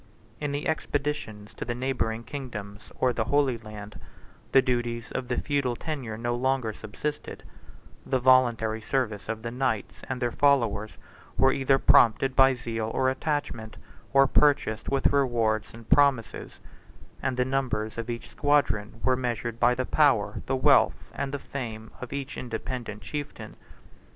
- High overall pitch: No, low, 125 Hz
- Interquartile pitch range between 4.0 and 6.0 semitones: No, average, 3.4 semitones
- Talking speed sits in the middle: Yes, average, 155 wpm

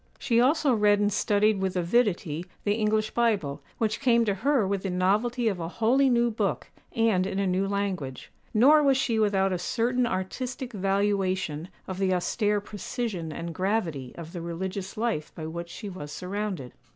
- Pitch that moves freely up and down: No, average, 4.0 semitones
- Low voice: No, high, 200 Hz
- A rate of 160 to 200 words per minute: Yes, average, 175 wpm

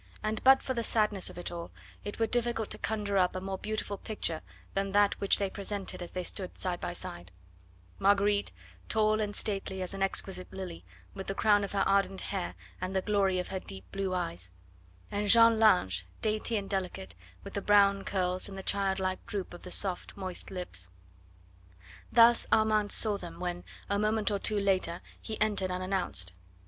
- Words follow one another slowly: No, average, 190 wpm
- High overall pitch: Yes, high, 195 Hz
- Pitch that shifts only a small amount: Yes, narrow, 2.2 semitones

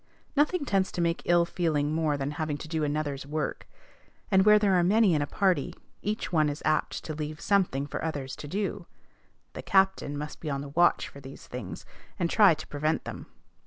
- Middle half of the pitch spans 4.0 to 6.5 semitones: Yes, average, 4.5 semitones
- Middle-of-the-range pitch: Yes, medium, 155 Hz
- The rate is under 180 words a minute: No, fast, 205 wpm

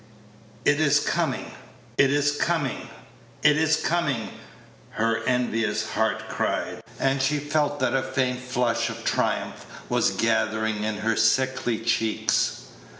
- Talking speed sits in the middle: No, slow, 130 wpm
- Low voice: Yes, low, 130 Hz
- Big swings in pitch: No, average, 4.3 semitones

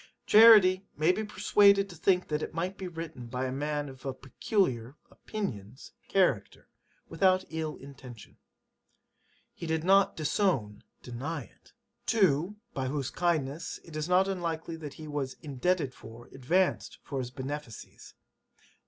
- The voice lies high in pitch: No, medium, 155 Hz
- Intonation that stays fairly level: No, wide, 5.6 semitones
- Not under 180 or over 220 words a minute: No, average, 145 wpm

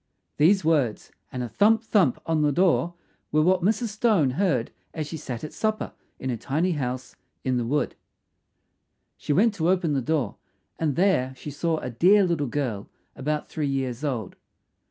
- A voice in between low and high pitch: Yes, medium, 150 Hz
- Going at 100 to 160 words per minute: No, average, 175 wpm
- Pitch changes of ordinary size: No, wide, 5.7 semitones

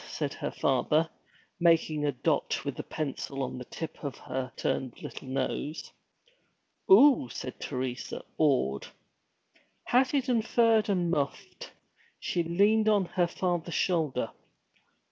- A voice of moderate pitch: Yes, medium, 160 Hz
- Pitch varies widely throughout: Yes, wide, 6.9 semitones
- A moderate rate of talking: No, slow, 125 wpm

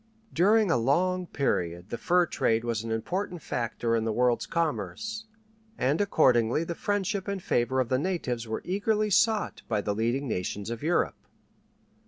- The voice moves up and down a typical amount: No, wide, 8.5 semitones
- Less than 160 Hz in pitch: Yes, medium, 140 Hz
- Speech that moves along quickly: No, average, 165 wpm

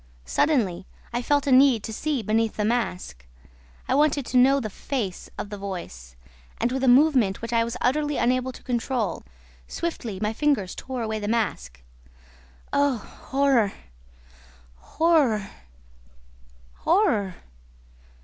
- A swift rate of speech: No, slow, 135 wpm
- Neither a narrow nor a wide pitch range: Yes, average, 4.9 semitones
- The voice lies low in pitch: No, high, 235 Hz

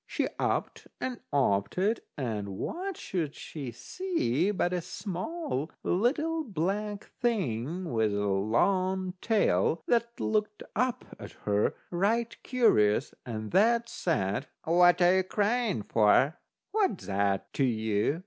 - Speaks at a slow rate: Yes, slow, 130 wpm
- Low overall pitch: No, medium, 180 Hz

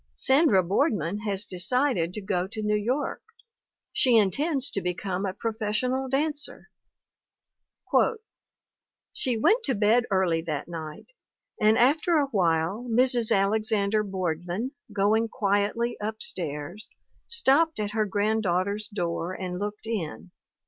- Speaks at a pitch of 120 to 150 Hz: No, high, 210 Hz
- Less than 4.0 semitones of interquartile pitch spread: No, average, 4.4 semitones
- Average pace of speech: No, slow, 125 wpm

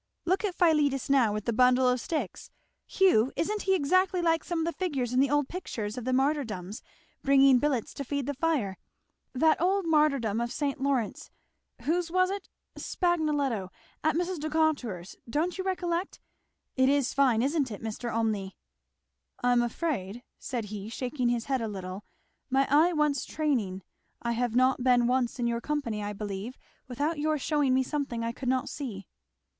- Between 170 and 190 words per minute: Yes, average, 175 wpm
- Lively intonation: No, average, 4.9 semitones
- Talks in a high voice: Yes, very high, 270 Hz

